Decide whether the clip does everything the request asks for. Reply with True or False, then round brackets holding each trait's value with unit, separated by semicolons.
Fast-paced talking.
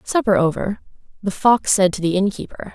False (175 wpm)